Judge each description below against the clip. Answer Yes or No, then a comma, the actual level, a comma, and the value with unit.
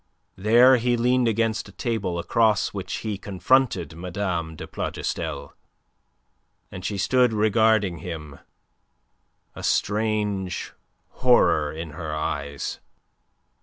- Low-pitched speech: Yes, low, 100 Hz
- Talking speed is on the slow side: Yes, slow, 105 wpm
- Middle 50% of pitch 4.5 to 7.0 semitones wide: Yes, average, 4.8 semitones